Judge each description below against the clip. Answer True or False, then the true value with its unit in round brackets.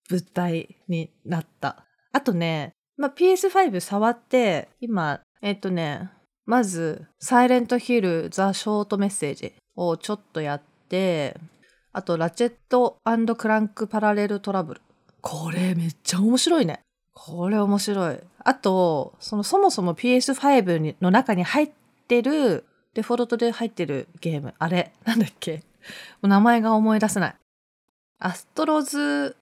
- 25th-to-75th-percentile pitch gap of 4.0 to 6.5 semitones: True (5.6 semitones)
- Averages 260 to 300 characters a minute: True (270 characters per minute)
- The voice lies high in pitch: True (205 Hz)